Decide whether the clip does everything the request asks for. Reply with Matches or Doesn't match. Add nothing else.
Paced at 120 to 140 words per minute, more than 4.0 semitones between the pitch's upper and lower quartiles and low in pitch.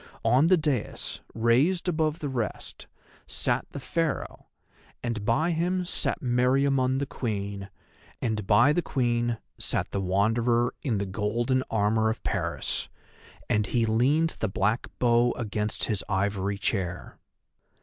Matches